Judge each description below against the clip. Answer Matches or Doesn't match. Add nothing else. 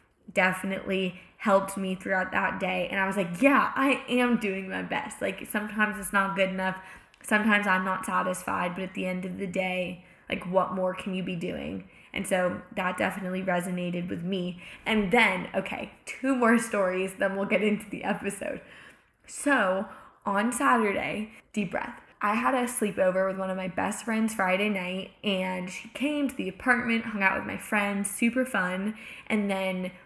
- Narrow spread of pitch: Matches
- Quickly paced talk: Doesn't match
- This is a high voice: Matches